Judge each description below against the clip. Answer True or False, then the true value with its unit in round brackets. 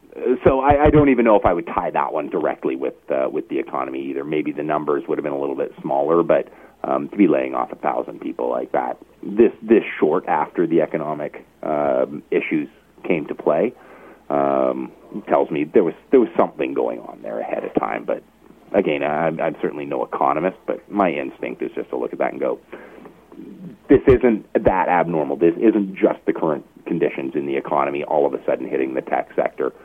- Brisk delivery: True (210 wpm)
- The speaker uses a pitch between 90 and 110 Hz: False (75 Hz)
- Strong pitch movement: True (7.5 semitones)